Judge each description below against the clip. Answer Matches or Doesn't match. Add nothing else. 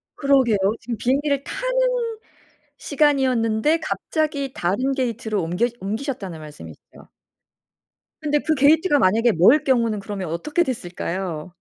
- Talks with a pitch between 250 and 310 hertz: Matches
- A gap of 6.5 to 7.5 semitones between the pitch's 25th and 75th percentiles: Matches